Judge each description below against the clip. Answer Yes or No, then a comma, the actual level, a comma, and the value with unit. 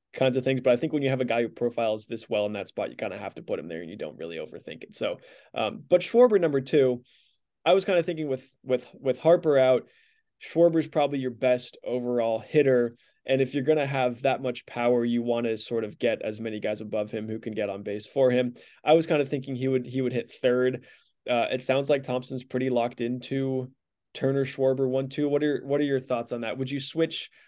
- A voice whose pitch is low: Yes, low, 130 Hz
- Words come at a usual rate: No, fast, 250 wpm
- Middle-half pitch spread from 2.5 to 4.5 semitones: Yes, average, 2.8 semitones